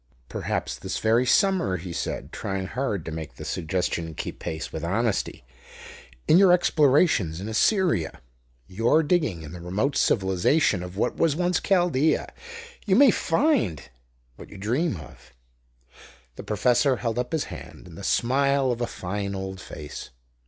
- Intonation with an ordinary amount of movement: No, wide, 8.8 semitones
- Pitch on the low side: Yes, low, 110 Hz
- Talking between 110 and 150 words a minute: No, average, 160 wpm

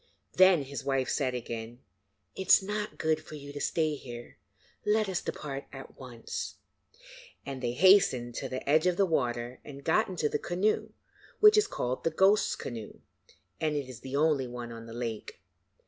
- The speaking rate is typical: Yes, average, 180 wpm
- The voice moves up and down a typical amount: No, wide, 6.1 semitones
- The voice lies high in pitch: No, medium, 140 Hz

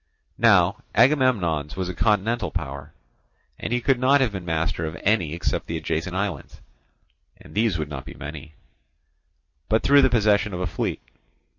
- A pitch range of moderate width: No, wide, 6.3 semitones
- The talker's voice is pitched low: Yes, very low, 95 Hz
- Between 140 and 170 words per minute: Yes, average, 165 wpm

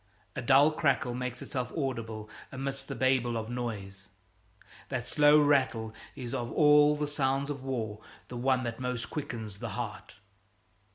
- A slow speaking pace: No, average, 155 wpm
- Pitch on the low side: Yes, low, 130 Hz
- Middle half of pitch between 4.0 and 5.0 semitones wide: No, average, 3.1 semitones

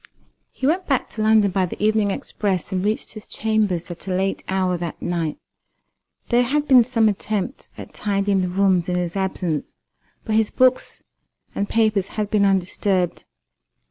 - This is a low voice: No, high, 200 Hz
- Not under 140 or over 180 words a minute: Yes, average, 170 wpm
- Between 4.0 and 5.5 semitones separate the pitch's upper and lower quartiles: No, average, 3.0 semitones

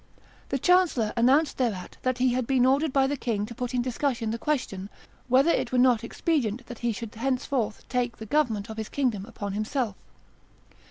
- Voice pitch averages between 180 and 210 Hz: No, high, 245 Hz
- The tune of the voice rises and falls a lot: No, average, 3.3 semitones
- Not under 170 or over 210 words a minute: Yes, average, 195 wpm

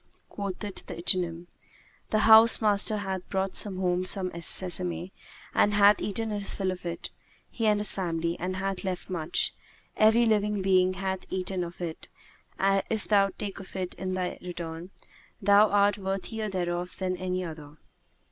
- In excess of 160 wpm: No, average, 155 wpm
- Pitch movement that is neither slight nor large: No, narrow, 2.2 semitones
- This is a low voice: No, high, 190 Hz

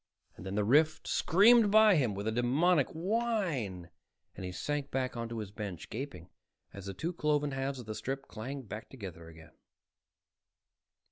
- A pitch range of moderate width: No, wide, 7.1 semitones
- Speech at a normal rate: Yes, average, 160 wpm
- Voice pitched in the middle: No, low, 130 Hz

